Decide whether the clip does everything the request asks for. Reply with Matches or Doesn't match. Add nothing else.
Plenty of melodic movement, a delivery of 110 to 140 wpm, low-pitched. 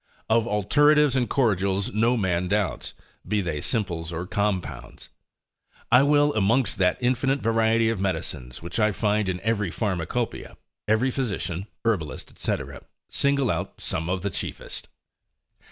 Doesn't match